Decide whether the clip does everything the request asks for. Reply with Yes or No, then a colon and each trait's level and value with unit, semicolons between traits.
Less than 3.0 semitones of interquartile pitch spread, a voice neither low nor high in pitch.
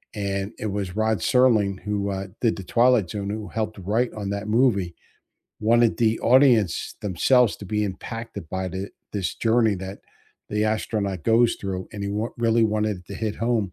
No: narrow, 2.5 semitones; low, 105 Hz